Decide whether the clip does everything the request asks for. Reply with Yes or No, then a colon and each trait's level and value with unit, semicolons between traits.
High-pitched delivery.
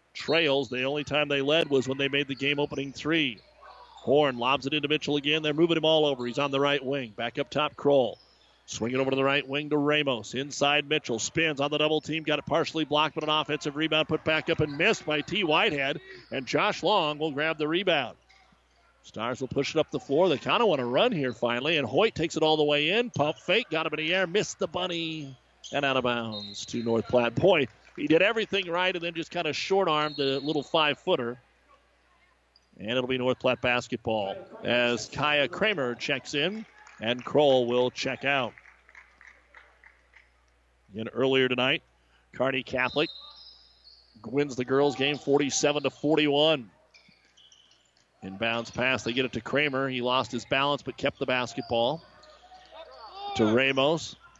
No: medium, 140 Hz